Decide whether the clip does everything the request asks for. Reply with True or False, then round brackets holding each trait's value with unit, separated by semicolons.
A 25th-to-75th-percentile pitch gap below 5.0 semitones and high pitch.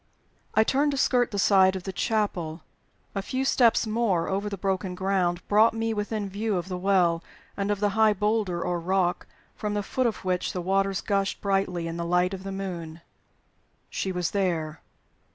True (2.8 semitones; 195 Hz)